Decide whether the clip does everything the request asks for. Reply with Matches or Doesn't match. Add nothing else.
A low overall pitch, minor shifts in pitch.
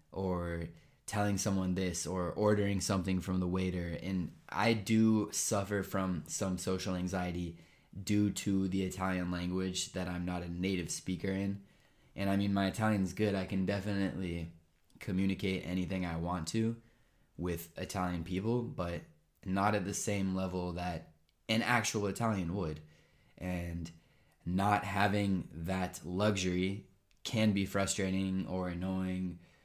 Matches